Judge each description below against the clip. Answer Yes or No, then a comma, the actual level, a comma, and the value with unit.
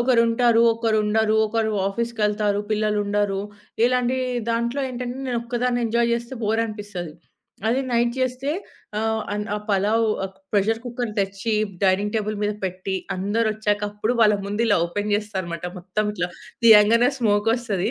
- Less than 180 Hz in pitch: No, high, 220 Hz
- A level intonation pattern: Yes, narrow, 2.2 semitones